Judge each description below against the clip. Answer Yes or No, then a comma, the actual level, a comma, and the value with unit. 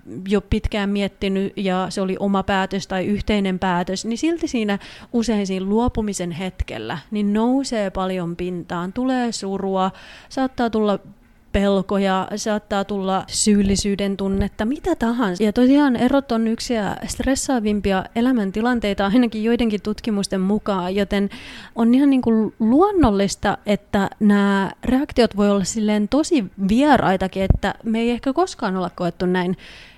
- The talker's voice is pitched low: No, high, 205 Hz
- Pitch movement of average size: Yes, average, 3.3 semitones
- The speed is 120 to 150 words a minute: Yes, average, 130 wpm